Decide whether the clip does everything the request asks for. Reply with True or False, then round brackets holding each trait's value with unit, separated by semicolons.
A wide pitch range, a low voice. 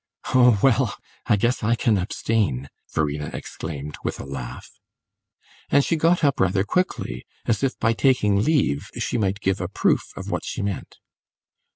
True (6.7 semitones; 105 Hz)